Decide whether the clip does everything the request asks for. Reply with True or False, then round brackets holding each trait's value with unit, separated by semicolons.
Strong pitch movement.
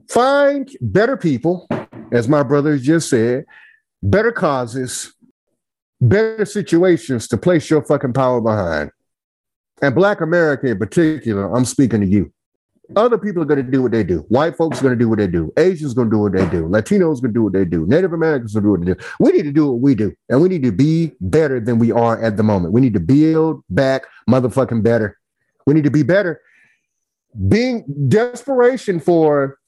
True (6.3 semitones)